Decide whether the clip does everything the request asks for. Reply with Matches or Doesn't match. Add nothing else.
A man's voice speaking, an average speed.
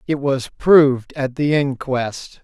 Matches